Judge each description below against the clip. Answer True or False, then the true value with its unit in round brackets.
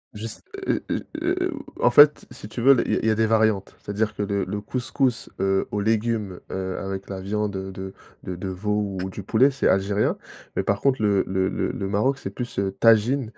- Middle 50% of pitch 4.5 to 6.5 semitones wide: False (2.9 semitones)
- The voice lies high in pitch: False (105 Hz)